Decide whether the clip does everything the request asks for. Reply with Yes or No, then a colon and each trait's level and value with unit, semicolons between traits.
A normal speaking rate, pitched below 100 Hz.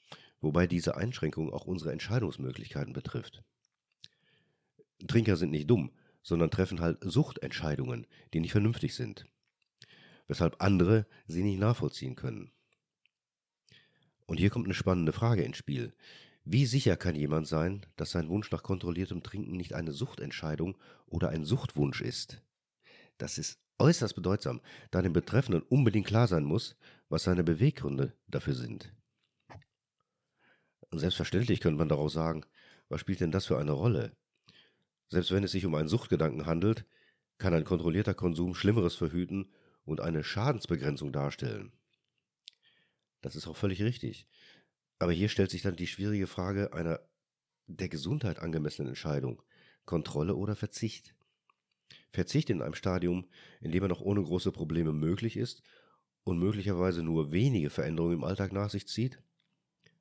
Yes: average, 140 wpm; very low, 90 Hz